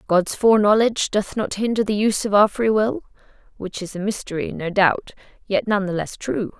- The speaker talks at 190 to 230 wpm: Yes, average, 200 wpm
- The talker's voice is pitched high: Yes, high, 205 Hz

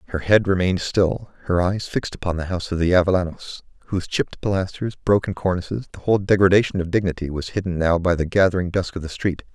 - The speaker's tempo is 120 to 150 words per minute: No, fast, 205 wpm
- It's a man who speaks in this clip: Yes, male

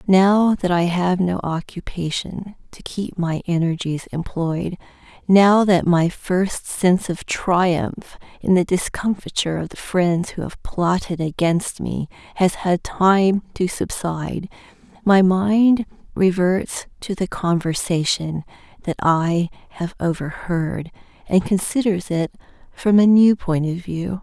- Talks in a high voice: No, medium, 180 Hz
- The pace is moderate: No, slow, 130 wpm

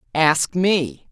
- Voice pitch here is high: No, medium, 170 Hz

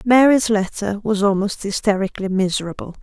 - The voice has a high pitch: Yes, high, 205 Hz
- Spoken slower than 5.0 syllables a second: No, 5.6 syllables/s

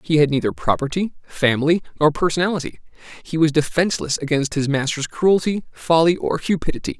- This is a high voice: No, medium, 160 Hz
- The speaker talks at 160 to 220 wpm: No, average, 145 wpm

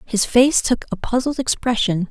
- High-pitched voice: Yes, high, 235 Hz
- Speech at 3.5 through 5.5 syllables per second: Yes, 4.7 syllables/s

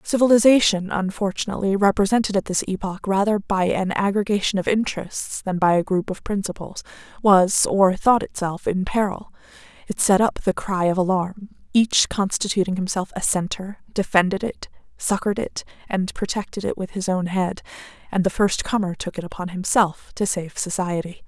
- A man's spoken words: No, female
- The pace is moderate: Yes, average, 165 wpm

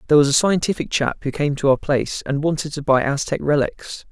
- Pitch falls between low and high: Yes, medium, 145 Hz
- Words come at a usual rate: No, fast, 235 wpm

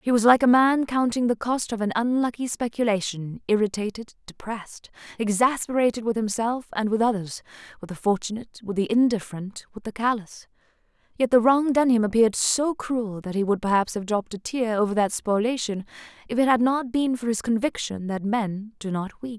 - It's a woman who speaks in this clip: Yes, female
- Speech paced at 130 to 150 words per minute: No, average, 185 wpm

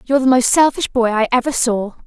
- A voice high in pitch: Yes, very high, 250 Hz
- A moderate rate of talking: No, fast, 235 wpm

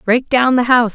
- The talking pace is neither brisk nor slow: No, fast, 255 wpm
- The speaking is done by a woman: Yes, female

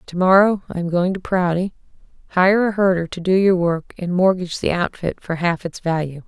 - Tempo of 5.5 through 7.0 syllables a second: No, 5.3 syllables/s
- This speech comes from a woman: Yes, female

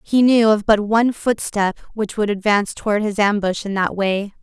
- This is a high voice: Yes, high, 210 Hz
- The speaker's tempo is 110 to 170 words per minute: No, fast, 205 wpm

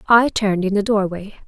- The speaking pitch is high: Yes, high, 205 Hz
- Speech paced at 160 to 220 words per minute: Yes, fast, 205 wpm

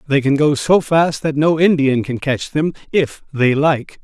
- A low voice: No, medium, 145 Hz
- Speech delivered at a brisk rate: No, average, 195 wpm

